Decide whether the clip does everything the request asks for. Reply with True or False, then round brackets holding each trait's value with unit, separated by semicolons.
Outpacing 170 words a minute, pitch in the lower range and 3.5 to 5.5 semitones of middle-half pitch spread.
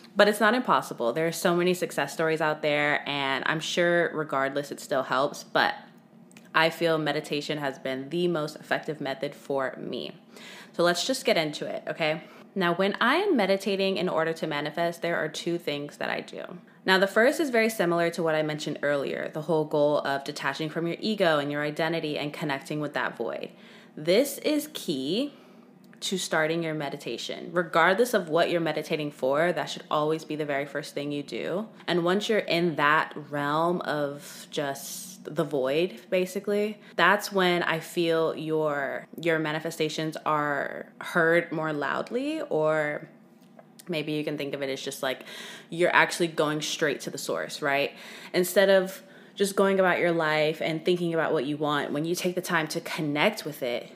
False (185 wpm; 165 Hz; 4.3 semitones)